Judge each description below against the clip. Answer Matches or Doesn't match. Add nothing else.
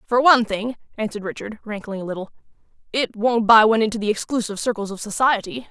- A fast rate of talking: Doesn't match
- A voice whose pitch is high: Matches